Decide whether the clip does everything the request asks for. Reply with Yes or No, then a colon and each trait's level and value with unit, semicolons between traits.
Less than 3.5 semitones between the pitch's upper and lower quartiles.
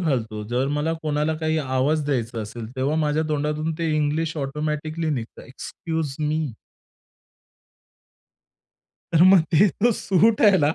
Yes: average, 2.8 semitones